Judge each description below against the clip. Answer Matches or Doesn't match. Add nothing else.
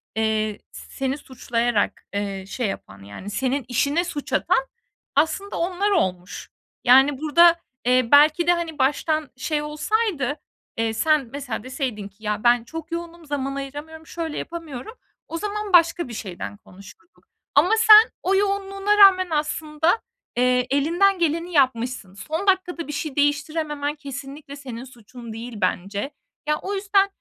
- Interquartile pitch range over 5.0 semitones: Matches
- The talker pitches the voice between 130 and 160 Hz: Doesn't match